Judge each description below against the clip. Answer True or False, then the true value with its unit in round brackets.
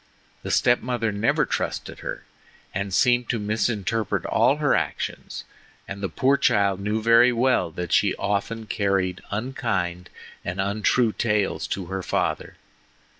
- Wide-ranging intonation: False (3.2 semitones)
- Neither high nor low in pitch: False (105 Hz)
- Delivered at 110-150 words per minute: True (140 wpm)